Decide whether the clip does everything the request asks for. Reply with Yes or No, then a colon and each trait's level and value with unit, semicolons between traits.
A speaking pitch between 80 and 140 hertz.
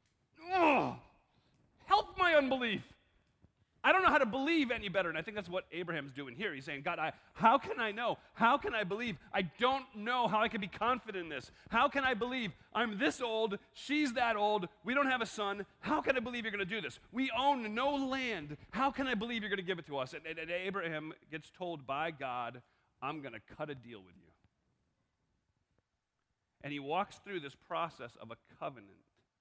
No: high, 205 Hz